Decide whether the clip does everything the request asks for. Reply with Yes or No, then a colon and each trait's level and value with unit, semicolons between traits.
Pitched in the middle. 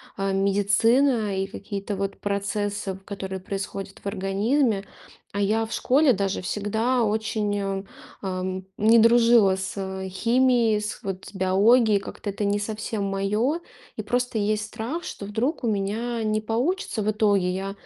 No: high, 205 Hz